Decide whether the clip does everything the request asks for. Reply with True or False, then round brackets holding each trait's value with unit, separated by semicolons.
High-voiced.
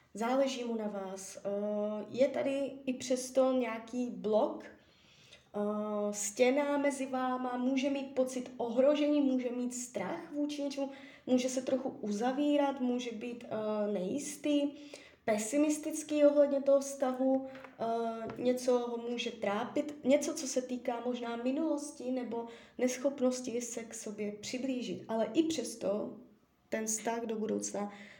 True (255 Hz)